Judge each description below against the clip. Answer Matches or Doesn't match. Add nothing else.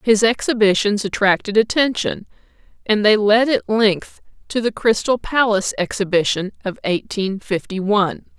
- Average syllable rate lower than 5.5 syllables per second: Matches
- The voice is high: Matches